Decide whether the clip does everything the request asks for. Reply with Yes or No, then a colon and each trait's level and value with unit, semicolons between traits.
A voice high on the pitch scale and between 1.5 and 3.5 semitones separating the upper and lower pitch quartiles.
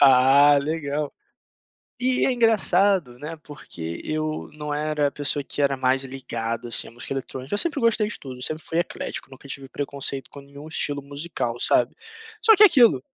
No: medium, 145 Hz; average, 3.2 semitones